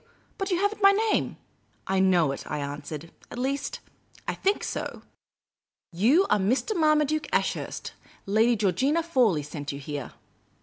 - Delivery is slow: No, average, 165 wpm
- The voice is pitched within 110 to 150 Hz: No, high, 230 Hz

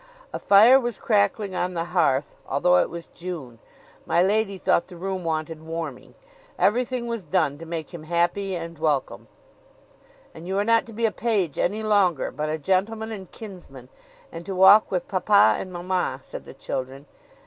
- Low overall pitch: No, medium, 180 Hz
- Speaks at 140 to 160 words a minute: No, average, 180 wpm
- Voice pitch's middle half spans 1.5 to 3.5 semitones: No, average, 3.9 semitones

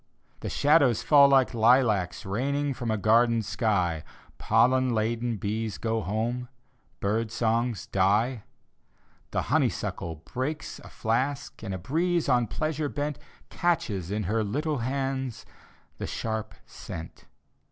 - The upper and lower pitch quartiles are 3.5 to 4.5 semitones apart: Yes, average, 3.8 semitones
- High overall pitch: No, low, 115 Hz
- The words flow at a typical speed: No, slow, 125 wpm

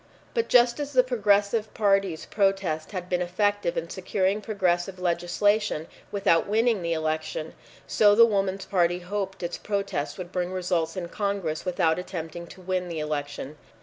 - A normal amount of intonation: Yes, average, 3.1 semitones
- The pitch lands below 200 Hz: Yes, medium, 185 Hz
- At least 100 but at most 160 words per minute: Yes, average, 155 wpm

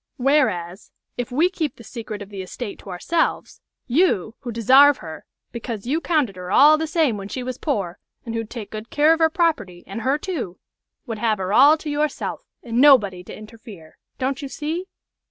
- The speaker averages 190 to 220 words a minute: Yes, average, 195 wpm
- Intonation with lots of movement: Yes, wide, 6.3 semitones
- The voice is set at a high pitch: Yes, high, 245 Hz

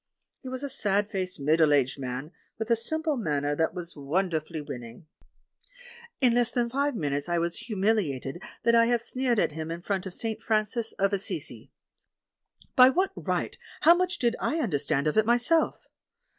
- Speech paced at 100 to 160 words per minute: No, average, 175 wpm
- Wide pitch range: Yes, wide, 7.4 semitones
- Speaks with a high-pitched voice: Yes, high, 200 Hz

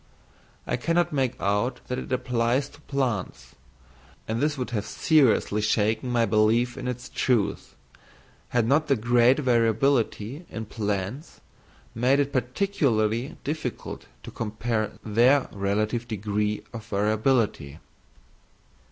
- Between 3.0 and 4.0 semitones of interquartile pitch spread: Yes, average, 3.6 semitones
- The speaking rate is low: Yes, slow, 120 wpm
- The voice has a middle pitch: No, low, 120 Hz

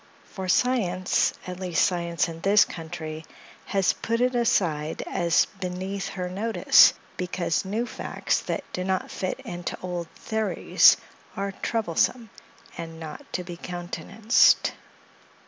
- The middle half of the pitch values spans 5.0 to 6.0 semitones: No, average, 2.8 semitones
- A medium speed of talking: No, slow, 130 wpm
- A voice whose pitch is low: No, medium, 185 Hz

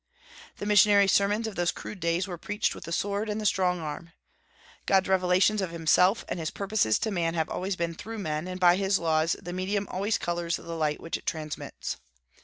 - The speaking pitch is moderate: Yes, medium, 180 Hz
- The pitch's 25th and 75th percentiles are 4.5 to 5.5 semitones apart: No, average, 3.1 semitones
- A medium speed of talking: No, fast, 210 wpm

